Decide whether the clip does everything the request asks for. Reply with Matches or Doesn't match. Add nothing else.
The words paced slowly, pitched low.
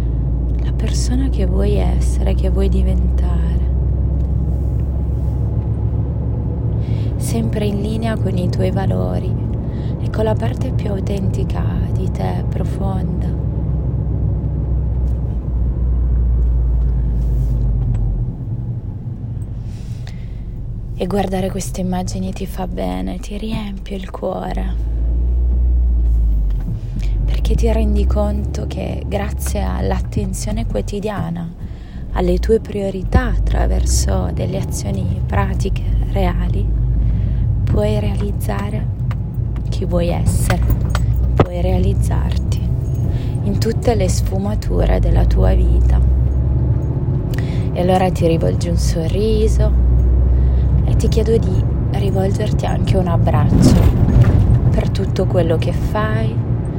Matches